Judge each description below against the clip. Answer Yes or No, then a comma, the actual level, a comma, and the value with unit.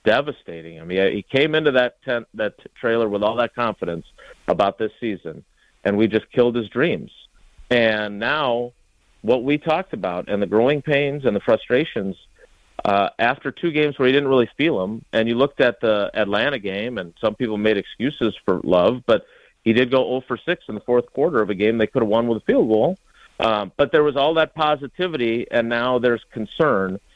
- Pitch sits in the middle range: No, low, 120 Hz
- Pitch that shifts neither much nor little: Yes, average, 4.0 semitones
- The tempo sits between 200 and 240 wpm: Yes, fast, 205 wpm